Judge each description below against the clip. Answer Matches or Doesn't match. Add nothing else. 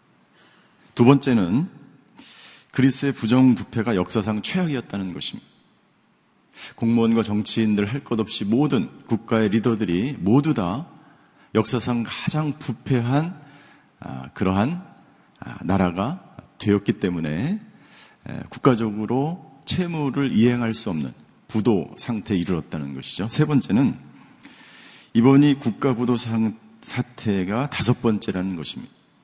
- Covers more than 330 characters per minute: Doesn't match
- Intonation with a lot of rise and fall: Doesn't match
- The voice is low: Matches